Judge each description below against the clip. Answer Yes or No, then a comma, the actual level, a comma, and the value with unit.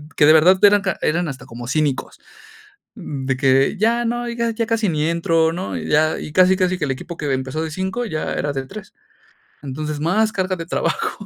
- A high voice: No, medium, 165 Hz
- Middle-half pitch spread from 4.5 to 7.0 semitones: Yes, wide, 5.4 semitones